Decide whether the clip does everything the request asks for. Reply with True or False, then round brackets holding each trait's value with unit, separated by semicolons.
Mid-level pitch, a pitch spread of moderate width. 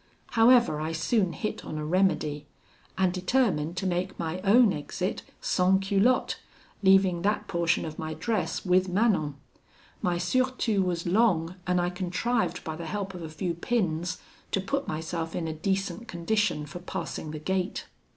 True (180 Hz; 3.4 semitones)